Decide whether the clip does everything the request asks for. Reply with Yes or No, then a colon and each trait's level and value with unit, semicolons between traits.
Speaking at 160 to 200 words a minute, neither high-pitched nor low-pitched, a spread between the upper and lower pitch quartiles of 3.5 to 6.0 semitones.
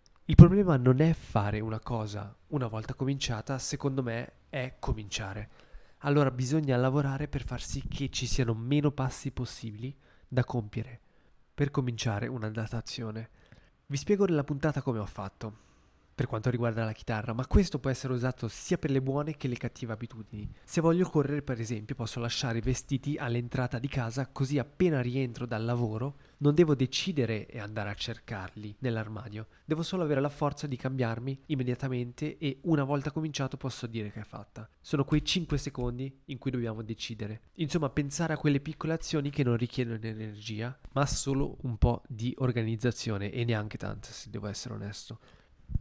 No: fast, 170 wpm; low, 125 Hz; average, 3.9 semitones